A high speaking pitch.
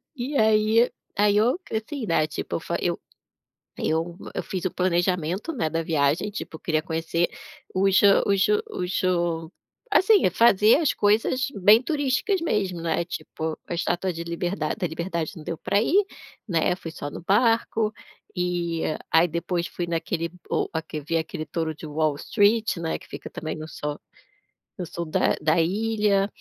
No: medium, 180 Hz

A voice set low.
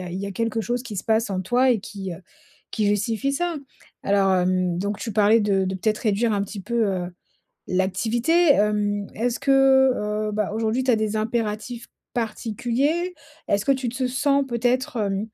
No: high, 220 Hz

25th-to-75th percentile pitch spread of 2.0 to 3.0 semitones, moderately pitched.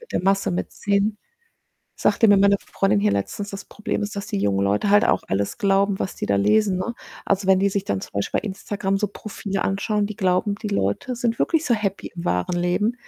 No: narrow, 2.5 semitones; high, 195 Hz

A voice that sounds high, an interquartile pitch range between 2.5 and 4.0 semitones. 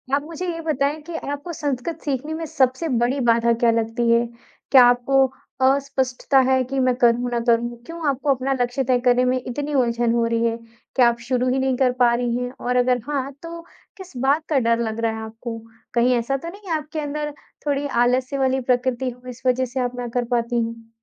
Yes: very high, 255 Hz; average, 2.8 semitones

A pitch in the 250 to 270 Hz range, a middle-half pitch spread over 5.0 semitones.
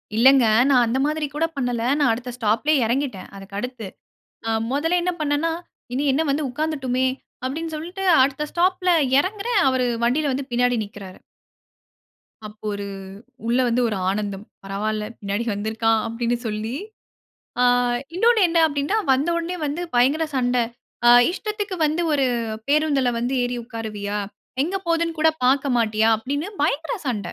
Yes: very high, 260 Hz; wide, 5.6 semitones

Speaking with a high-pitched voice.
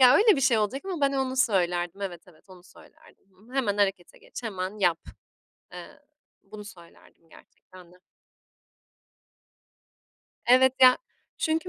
Yes: high, 210 Hz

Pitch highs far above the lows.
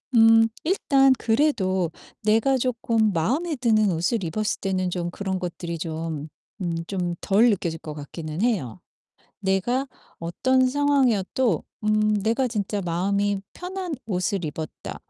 Yes: wide, 5.7 semitones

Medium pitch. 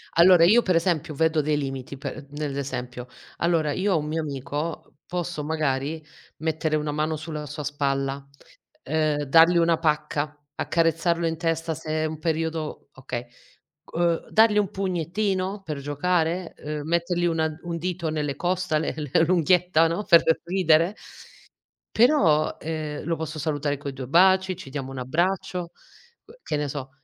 Yes: medium, 160 Hz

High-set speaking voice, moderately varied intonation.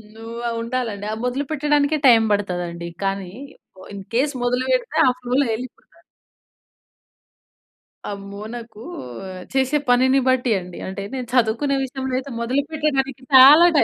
Yes: very high, 250 Hz; average, 3.6 semitones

